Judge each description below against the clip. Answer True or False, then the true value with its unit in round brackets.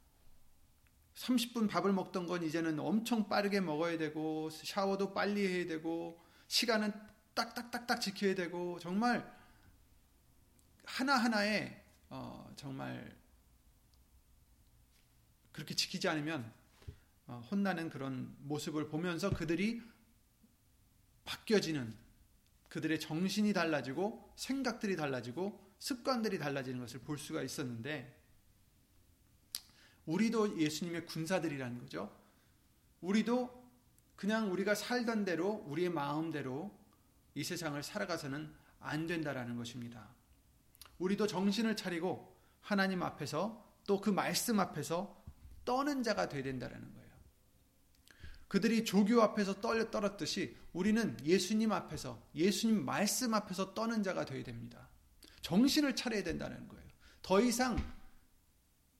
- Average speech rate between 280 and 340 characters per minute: False (260 characters per minute)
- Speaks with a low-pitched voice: False (175 Hz)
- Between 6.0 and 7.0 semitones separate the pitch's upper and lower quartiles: True (6.4 semitones)